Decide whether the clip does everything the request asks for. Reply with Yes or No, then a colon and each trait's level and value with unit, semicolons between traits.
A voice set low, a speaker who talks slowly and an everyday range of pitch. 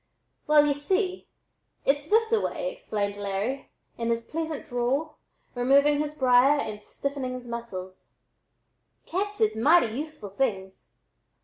No: very high, 275 Hz; slow, 130 wpm; average, 4.9 semitones